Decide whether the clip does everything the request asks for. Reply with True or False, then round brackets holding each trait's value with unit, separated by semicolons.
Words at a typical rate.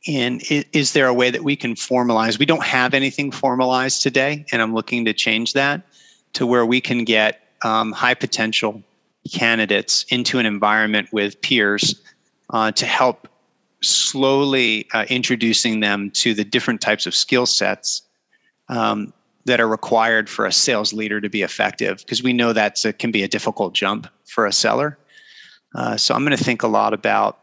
True (175 wpm)